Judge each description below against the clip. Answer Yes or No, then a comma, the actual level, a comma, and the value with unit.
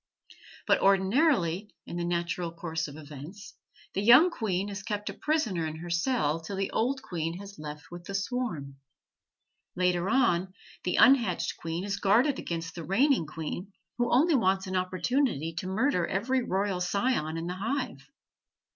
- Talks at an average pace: Yes, average, 165 wpm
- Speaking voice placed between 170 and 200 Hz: Yes, high, 190 Hz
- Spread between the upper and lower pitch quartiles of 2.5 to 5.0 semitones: No, wide, 5.4 semitones